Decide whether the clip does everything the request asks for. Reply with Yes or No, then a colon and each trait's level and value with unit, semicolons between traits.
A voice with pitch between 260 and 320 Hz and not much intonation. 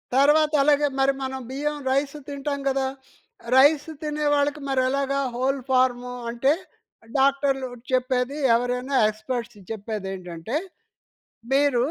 Yes: very high, 270 Hz; narrow, 2.3 semitones